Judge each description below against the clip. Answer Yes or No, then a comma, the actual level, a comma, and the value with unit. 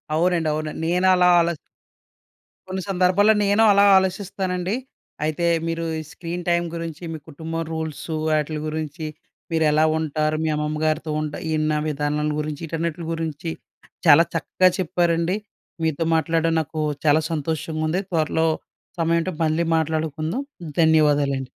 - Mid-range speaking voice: Yes, medium, 160 Hz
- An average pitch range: No, narrow, 2.0 semitones